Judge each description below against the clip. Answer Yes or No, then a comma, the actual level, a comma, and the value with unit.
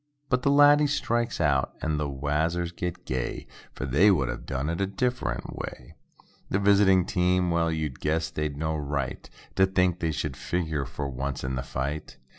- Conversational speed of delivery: Yes, average, 180 wpm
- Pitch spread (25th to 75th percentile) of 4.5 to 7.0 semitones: Yes, average, 5.0 semitones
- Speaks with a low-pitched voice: Yes, very low, 80 Hz